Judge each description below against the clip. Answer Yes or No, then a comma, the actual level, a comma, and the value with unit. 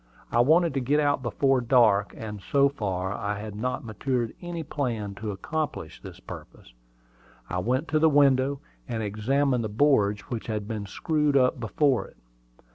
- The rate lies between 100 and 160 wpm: No, average, 170 wpm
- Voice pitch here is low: Yes, low, 125 Hz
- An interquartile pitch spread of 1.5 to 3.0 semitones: No, average, 5.2 semitones